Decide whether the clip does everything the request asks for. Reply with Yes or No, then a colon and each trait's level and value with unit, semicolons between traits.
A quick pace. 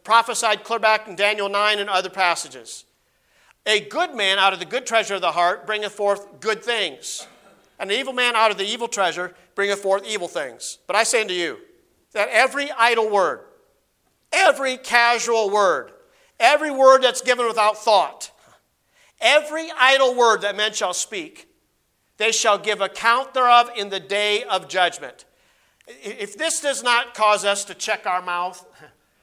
No: average, 165 wpm